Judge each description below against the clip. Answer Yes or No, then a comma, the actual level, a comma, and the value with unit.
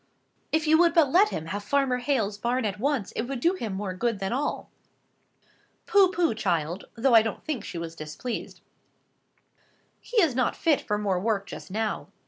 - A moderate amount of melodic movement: No, wide, 6.5 semitones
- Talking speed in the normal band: Yes, average, 190 wpm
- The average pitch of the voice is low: No, high, 235 Hz